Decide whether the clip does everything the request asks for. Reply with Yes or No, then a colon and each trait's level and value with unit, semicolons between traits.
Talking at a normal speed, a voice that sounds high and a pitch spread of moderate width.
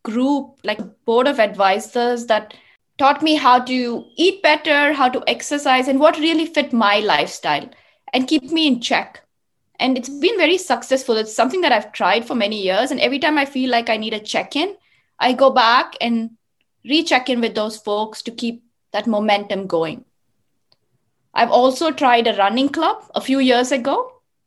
Yes: average, 180 wpm; very high, 255 Hz; average, 4.4 semitones